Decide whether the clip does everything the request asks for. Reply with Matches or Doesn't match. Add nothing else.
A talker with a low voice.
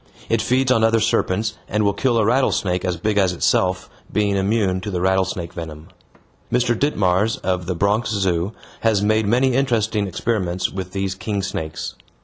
Matches